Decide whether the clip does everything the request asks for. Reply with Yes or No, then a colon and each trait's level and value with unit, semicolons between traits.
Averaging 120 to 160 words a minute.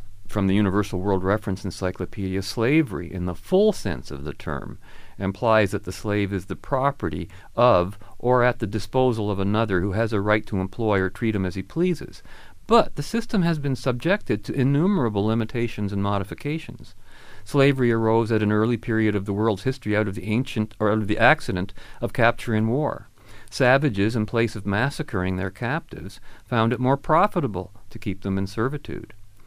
No: average, 185 wpm